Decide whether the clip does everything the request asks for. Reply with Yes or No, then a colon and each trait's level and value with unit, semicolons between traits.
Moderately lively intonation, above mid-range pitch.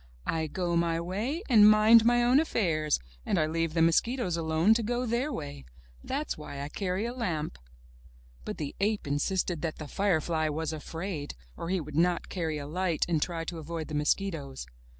No: average, 5.0 semitones; medium, 170 Hz